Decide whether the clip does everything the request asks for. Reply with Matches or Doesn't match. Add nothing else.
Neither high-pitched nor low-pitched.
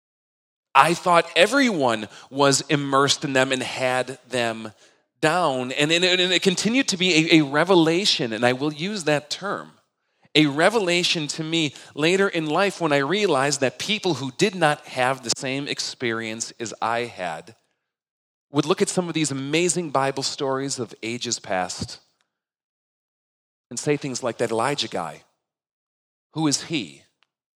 Matches